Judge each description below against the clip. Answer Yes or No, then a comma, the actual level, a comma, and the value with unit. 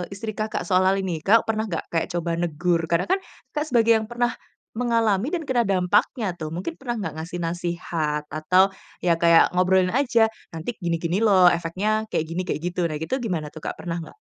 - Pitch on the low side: No, medium, 185 Hz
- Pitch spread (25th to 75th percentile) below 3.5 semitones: No, average, 4.7 semitones